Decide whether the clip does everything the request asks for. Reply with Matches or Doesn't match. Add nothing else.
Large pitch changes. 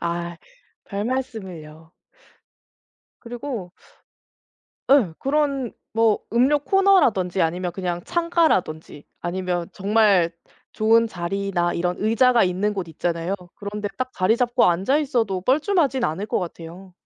Matches